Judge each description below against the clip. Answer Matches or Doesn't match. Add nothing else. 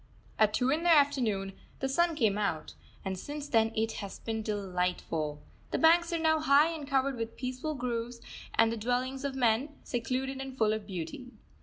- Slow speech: Doesn't match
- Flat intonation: Doesn't match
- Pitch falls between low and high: Doesn't match